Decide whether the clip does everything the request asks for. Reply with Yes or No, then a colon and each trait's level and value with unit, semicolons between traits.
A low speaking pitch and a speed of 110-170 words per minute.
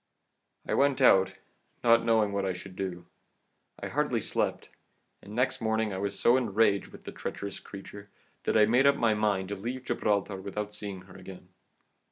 No: low, 105 Hz; average, 180 wpm